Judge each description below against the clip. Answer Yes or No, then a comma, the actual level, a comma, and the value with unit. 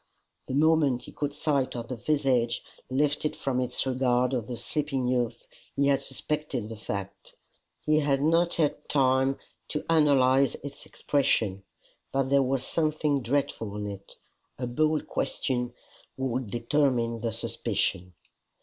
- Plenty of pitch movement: No, average, 3.1 semitones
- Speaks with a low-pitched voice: Yes, low, 130 Hz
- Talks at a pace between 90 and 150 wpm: Yes, average, 140 wpm